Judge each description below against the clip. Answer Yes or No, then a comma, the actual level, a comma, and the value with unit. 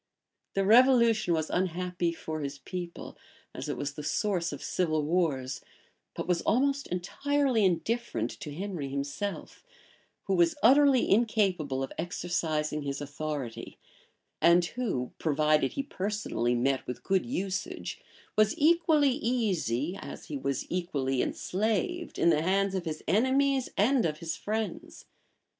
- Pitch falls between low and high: Yes, medium, 180 Hz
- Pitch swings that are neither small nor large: No, wide, 6.7 semitones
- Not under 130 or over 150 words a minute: Yes, slow, 135 wpm